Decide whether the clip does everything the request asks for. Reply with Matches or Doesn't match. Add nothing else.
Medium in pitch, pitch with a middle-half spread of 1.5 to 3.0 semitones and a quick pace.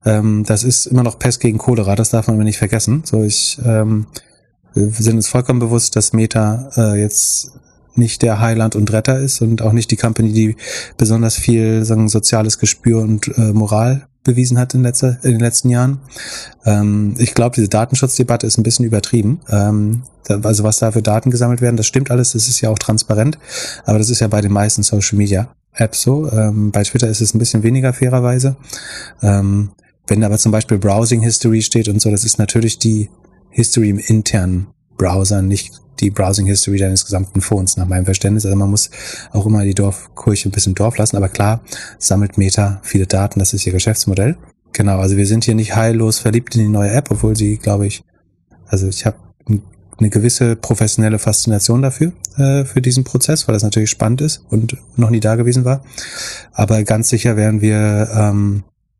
Doesn't match